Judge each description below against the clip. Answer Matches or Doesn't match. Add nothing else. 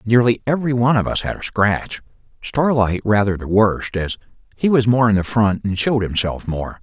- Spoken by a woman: Doesn't match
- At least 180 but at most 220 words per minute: Matches